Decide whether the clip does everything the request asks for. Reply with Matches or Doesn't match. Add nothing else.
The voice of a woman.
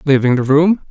Doesn't match